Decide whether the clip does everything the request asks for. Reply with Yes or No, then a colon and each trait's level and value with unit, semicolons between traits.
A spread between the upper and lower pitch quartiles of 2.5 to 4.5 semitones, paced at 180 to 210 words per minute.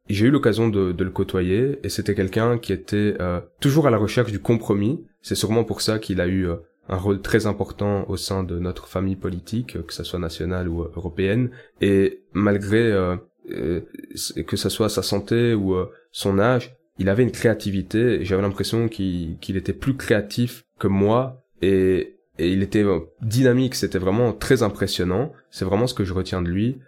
Yes: average, 3.4 semitones; average, 195 wpm